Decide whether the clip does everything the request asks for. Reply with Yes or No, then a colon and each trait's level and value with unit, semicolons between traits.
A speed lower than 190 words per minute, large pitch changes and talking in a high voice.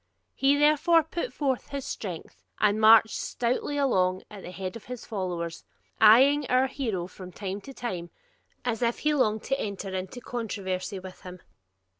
Yes: average, 165 wpm; wide, 6.2 semitones; high, 220 Hz